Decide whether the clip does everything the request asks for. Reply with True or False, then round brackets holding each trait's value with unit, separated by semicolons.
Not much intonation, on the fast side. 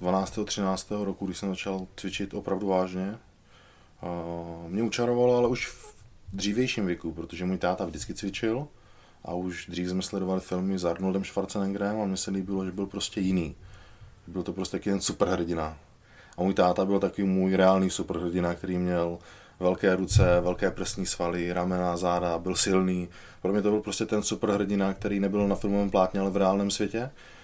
True (2.0 semitones; 175 wpm)